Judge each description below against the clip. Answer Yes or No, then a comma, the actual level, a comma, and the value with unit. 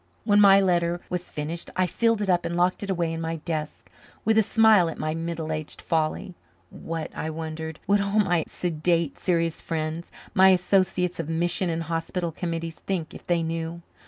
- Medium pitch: Yes, medium, 170 Hz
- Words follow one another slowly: No, average, 190 wpm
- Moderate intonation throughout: No, narrow, 2.1 semitones